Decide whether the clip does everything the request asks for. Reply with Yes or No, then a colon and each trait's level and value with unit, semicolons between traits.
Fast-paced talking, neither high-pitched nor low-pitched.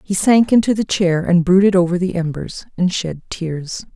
No: average, 195 wpm; medium, 180 Hz